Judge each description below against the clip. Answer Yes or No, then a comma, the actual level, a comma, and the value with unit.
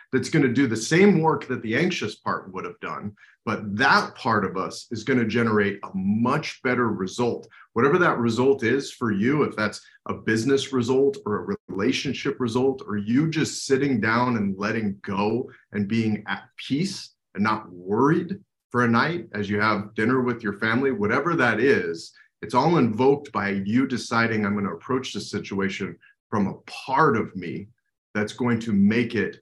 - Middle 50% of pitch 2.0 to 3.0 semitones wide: No, average, 4.2 semitones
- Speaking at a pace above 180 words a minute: Yes, average, 190 wpm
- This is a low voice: Yes, low, 115 Hz